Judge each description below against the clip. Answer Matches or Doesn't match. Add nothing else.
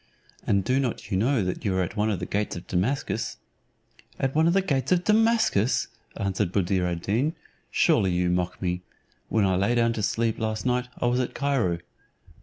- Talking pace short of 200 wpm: Doesn't match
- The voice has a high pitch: Doesn't match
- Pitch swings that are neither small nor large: Doesn't match